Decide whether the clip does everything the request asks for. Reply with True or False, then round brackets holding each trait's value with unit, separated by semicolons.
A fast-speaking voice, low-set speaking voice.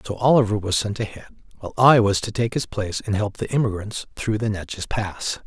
True (220 wpm; 105 Hz)